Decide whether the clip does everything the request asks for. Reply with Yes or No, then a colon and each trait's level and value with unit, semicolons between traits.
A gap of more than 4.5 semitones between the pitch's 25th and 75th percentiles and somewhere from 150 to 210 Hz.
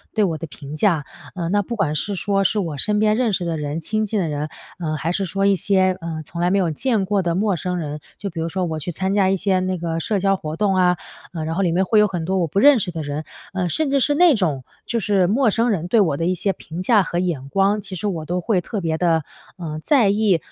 No: average, 3.8 semitones; medium, 185 Hz